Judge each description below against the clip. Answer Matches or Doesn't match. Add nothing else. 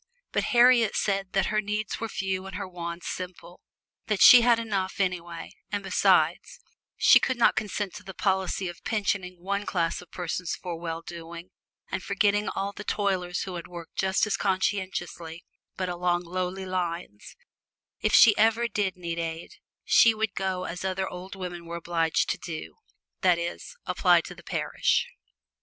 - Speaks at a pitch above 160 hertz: Matches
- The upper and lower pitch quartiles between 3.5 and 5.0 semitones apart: Doesn't match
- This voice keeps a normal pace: Matches